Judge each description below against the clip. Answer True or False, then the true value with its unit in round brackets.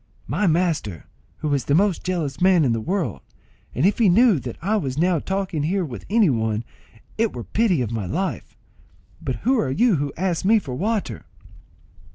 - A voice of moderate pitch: True (170 Hz)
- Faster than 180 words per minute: True (195 wpm)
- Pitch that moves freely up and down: True (6.7 semitones)